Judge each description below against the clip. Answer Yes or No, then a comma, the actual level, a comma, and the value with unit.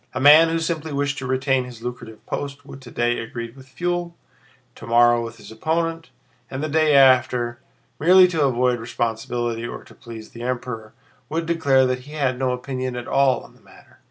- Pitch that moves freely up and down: No, average, 3.7 semitones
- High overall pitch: No, low, 130 Hz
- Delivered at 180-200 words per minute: Yes, average, 185 wpm